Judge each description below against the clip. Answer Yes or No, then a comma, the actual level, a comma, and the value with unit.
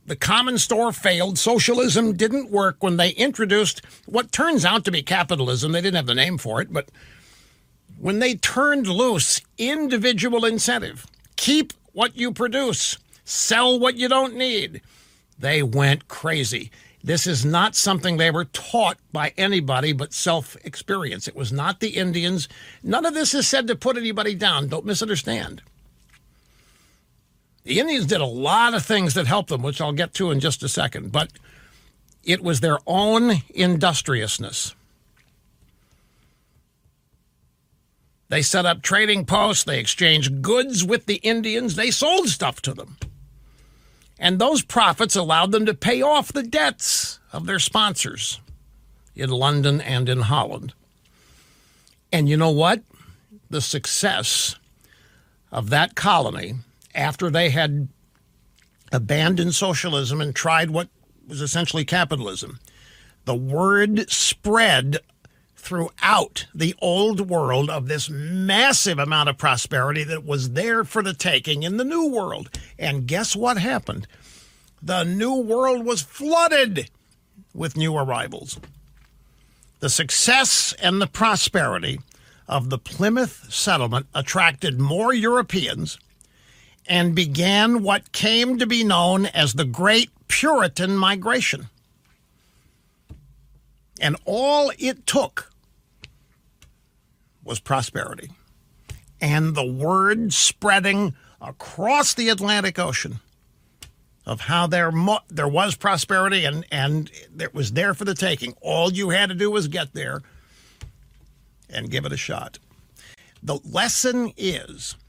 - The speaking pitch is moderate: Yes, medium, 175 Hz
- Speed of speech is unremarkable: No, slow, 130 wpm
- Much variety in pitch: Yes, wide, 7.5 semitones